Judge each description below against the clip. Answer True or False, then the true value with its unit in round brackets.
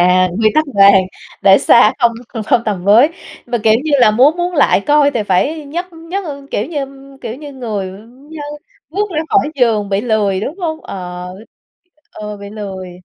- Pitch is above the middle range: True (235 Hz)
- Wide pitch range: True (6.9 semitones)